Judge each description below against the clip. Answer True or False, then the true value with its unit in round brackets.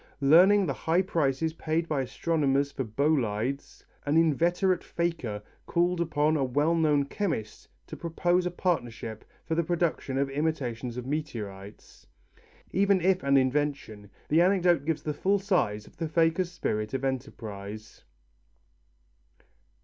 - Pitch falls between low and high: True (150 Hz)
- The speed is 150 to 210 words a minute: False (135 wpm)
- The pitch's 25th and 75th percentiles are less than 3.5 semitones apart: False (4.7 semitones)